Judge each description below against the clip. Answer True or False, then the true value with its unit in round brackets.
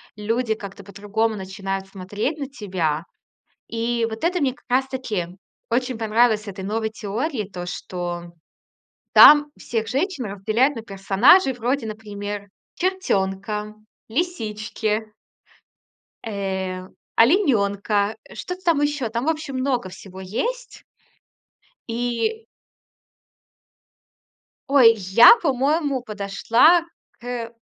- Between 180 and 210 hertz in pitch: False (225 Hz)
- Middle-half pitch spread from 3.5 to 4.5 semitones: False (4.9 semitones)